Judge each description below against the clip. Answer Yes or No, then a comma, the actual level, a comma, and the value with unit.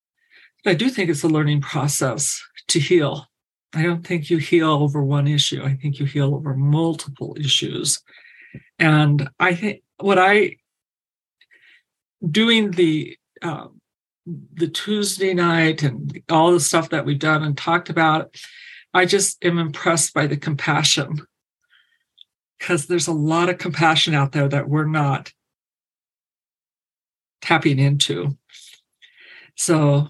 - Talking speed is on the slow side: Yes, slow, 130 wpm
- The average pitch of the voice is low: No, medium, 160 Hz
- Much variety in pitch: No, average, 3.3 semitones